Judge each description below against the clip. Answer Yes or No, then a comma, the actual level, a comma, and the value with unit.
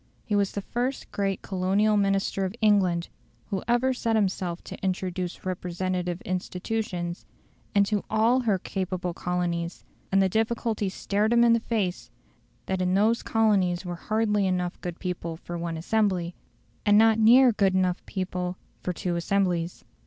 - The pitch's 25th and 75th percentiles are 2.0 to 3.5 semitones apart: Yes, average, 3.2 semitones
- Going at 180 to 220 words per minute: No, average, 155 wpm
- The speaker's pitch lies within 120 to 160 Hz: No, high, 190 Hz